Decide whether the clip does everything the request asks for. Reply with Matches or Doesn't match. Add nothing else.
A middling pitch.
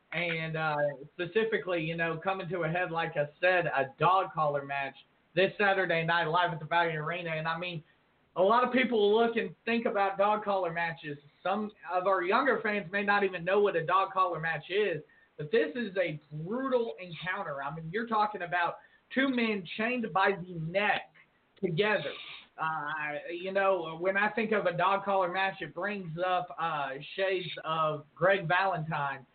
Matches